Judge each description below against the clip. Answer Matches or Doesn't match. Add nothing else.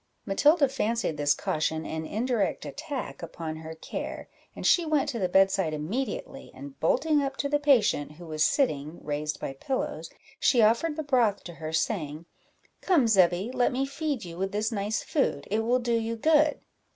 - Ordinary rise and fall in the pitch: Doesn't match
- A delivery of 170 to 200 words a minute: Matches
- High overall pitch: Matches